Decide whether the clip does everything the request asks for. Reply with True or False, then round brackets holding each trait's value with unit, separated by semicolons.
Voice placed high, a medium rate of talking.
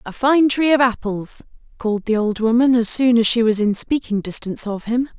False (230 Hz; 220 wpm)